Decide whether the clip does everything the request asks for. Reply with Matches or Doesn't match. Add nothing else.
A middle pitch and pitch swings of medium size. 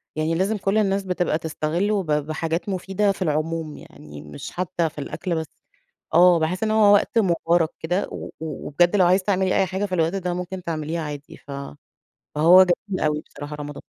Matches